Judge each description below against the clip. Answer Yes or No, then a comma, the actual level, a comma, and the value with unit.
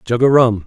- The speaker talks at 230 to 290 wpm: Yes, fast, 270 wpm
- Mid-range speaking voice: No, low, 120 Hz